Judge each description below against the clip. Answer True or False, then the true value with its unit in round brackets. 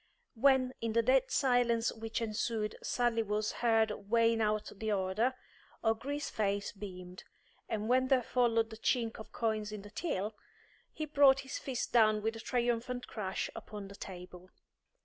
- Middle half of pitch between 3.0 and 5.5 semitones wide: False (2.6 semitones)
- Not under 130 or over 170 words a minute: True (160 wpm)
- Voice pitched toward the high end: True (225 Hz)